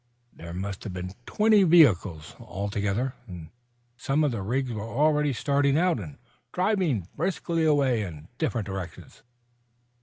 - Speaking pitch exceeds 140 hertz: No, low, 120 Hz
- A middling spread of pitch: No, wide, 8.0 semitones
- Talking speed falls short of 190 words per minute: Yes, average, 140 wpm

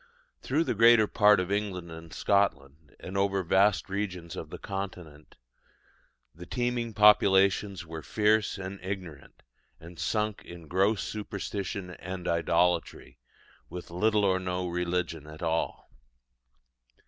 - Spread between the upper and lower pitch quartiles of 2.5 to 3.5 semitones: Yes, average, 3.2 semitones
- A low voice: Yes, very low, 95 Hz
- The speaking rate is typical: No, slow, 130 wpm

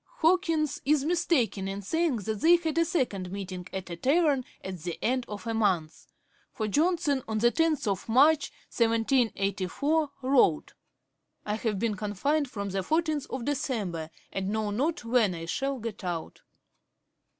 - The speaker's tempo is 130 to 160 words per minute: Yes, average, 150 wpm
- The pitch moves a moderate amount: No, wide, 7.1 semitones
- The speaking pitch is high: Yes, high, 230 Hz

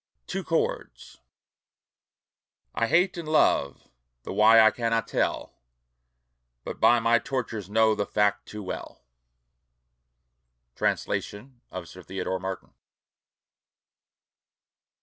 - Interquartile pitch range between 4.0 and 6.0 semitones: No, average, 3.4 semitones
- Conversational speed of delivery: No, slow, 100 wpm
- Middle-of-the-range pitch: No, low, 110 Hz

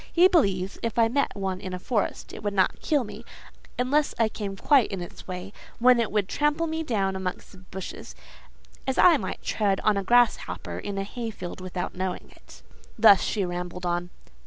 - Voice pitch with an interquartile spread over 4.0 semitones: Yes, average, 4.6 semitones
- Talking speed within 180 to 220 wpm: Yes, average, 195 wpm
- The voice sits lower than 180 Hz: No, high, 200 Hz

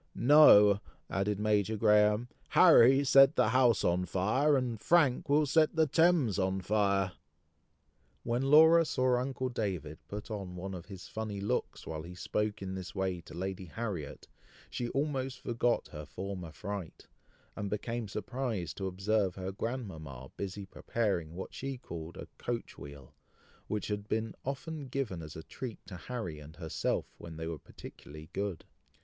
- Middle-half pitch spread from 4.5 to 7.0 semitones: Yes, wide, 5.5 semitones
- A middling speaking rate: Yes, average, 160 wpm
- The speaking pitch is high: No, low, 105 Hz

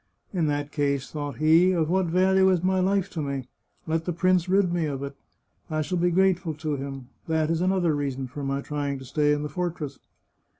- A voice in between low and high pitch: Yes, medium, 160 Hz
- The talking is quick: Yes, fast, 215 wpm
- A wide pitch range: No, average, 3.9 semitones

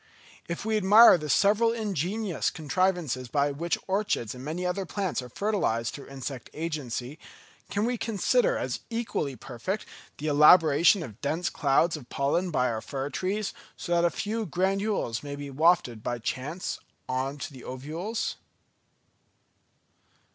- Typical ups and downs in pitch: No, wide, 6.4 semitones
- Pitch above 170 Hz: No, medium, 165 Hz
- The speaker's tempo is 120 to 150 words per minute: Yes, average, 145 wpm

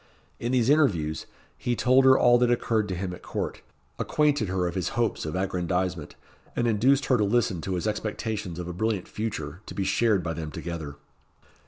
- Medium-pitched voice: No, low, 100 Hz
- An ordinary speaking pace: Yes, average, 195 wpm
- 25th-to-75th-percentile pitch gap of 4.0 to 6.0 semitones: Yes, average, 5.1 semitones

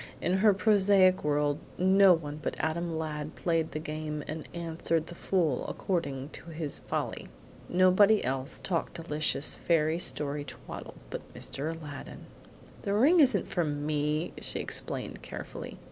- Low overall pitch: No, medium, 160 Hz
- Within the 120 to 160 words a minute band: Yes, average, 145 wpm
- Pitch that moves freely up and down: No, average, 3.5 semitones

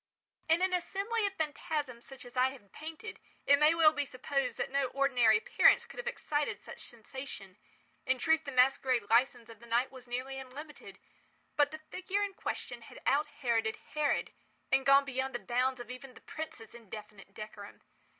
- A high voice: Yes, very high, 265 Hz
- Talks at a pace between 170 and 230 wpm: Yes, average, 180 wpm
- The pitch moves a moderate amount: Yes, average, 3.9 semitones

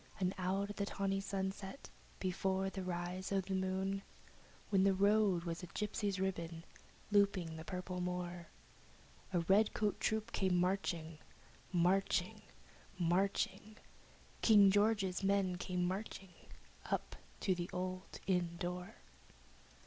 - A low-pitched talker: No, high, 190 Hz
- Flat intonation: Yes, narrow, 1.7 semitones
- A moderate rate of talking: No, slow, 125 wpm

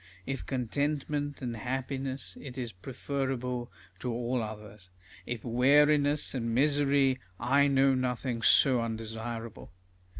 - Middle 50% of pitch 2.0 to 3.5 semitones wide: Yes, average, 2.9 semitones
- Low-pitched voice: Yes, low, 130 Hz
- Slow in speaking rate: Yes, slow, 110 wpm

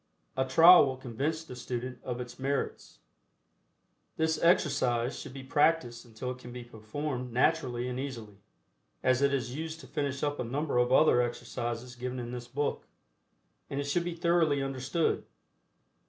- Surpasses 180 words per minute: No, average, 165 wpm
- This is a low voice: Yes, low, 130 Hz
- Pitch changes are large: No, average, 3.1 semitones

